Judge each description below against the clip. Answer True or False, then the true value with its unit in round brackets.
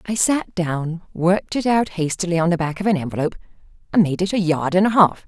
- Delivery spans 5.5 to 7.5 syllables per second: True (6.0 syllables/s)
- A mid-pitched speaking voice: True (180 Hz)